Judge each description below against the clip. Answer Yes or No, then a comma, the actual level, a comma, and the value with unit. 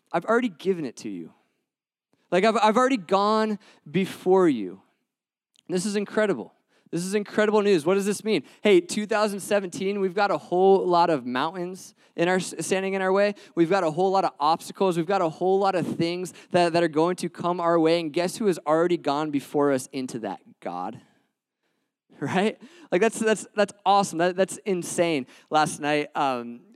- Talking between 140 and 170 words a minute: No, average, 190 wpm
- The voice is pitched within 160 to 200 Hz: Yes, high, 190 Hz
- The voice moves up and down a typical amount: Yes, average, 3.5 semitones